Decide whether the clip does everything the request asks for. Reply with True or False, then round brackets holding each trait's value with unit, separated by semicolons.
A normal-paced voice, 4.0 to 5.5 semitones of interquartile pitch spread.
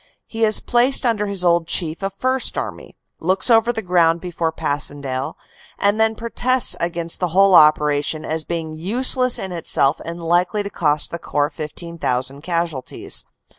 True (160 wpm; 4.8 semitones)